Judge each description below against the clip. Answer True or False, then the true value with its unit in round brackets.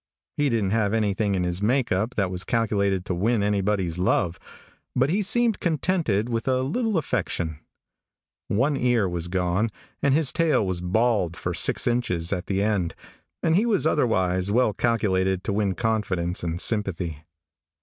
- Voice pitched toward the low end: True (105 Hz)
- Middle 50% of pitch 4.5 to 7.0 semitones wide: True (5.1 semitones)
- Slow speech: False (165 wpm)